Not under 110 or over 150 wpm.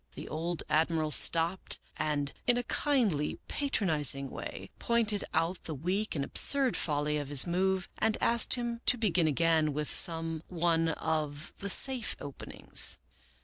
Yes: average, 145 wpm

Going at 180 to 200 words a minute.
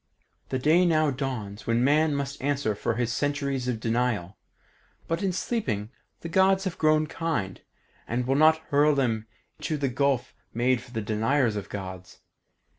No: average, 160 wpm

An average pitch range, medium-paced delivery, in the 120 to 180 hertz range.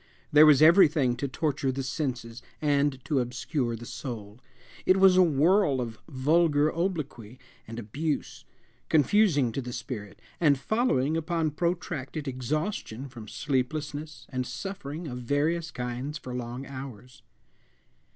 No: average, 4.1 semitones; slow, 130 wpm; medium, 140 Hz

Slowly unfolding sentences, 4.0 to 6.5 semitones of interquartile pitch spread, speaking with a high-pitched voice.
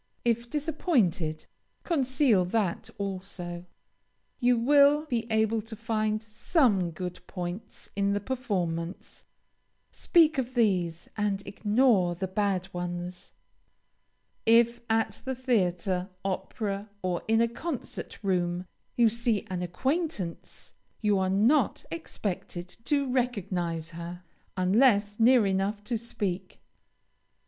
Yes: slow, 110 wpm; average, 4.7 semitones; high, 205 Hz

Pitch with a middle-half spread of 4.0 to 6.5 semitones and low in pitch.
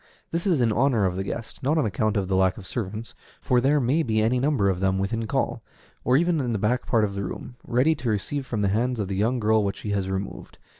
Yes: average, 4.3 semitones; low, 110 Hz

